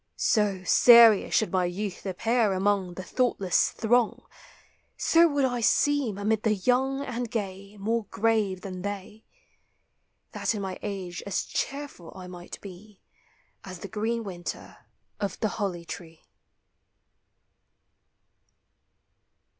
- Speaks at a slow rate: Yes, slow, 120 wpm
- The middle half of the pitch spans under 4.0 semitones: Yes, average, 3.6 semitones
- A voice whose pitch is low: No, high, 205 Hz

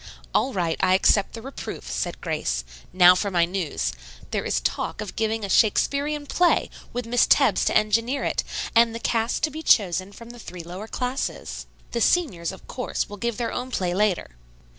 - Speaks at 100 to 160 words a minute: No, average, 190 wpm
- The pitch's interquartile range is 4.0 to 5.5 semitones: Yes, average, 5.1 semitones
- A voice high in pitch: Yes, high, 215 Hz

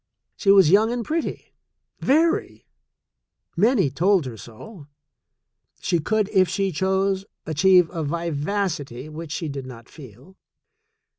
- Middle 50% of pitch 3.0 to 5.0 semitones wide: No, wide, 5.4 semitones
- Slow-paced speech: Yes, slow, 125 wpm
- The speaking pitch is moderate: Yes, medium, 180 Hz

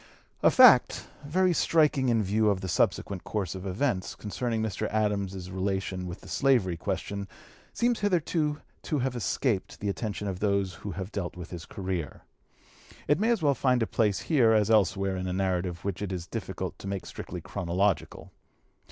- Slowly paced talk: No, average, 180 wpm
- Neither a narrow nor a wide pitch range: Yes, average, 4.7 semitones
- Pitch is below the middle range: Yes, low, 100 Hz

